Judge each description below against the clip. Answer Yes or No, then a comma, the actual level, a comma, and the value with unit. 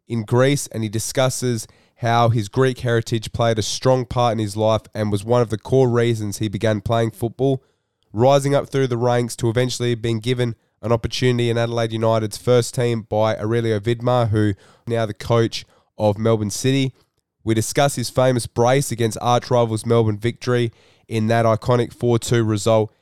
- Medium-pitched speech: No, low, 115 Hz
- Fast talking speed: No, average, 175 wpm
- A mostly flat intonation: Yes, narrow, 1.8 semitones